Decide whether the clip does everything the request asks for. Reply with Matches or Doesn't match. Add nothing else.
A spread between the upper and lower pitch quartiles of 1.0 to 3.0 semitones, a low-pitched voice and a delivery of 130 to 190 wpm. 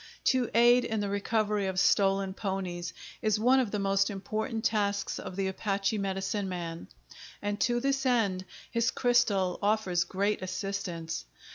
Doesn't match